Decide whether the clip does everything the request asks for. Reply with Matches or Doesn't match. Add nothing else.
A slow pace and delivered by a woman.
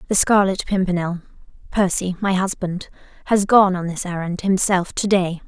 Matches